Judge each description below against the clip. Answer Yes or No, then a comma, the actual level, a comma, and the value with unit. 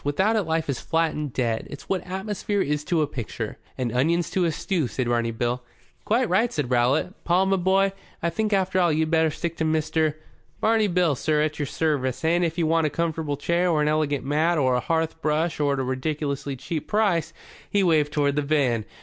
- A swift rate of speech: Yes, fast, 220 wpm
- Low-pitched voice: No, medium, 155 Hz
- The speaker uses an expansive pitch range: No, average, 3.5 semitones